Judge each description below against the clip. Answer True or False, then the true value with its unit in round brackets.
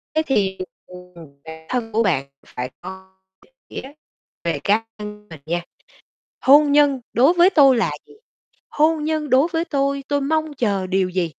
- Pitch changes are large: True (7.6 semitones)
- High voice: True (240 Hz)